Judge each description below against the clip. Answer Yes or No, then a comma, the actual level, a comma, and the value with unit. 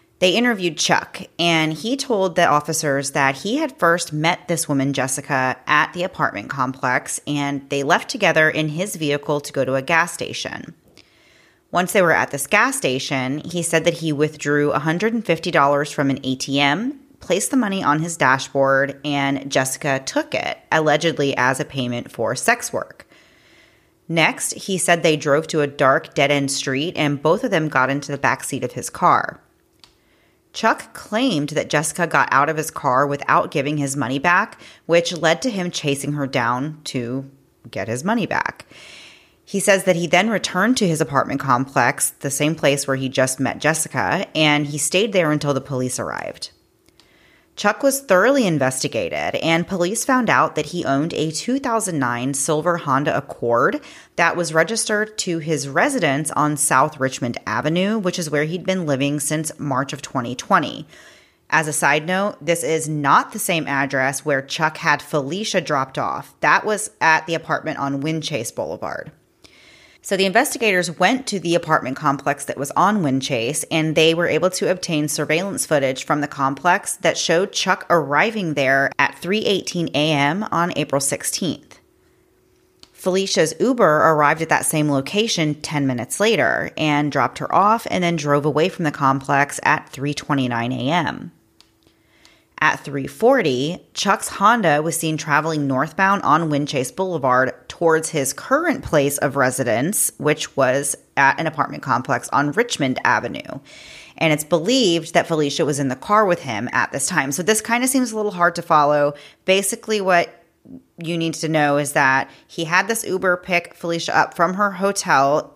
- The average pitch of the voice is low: No, medium, 155 Hz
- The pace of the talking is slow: No, average, 170 wpm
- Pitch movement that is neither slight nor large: Yes, average, 4.0 semitones